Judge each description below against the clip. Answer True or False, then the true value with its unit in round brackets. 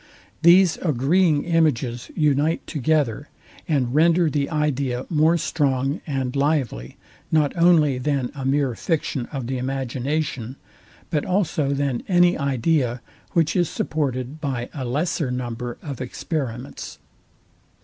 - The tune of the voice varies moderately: True (3.7 semitones)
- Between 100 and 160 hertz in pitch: True (140 Hz)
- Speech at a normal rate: False (120 wpm)